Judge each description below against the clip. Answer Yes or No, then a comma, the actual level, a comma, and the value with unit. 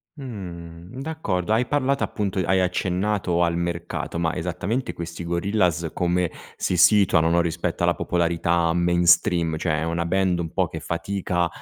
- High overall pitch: No, very low, 85 Hz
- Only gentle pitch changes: Yes, narrow, 2.3 semitones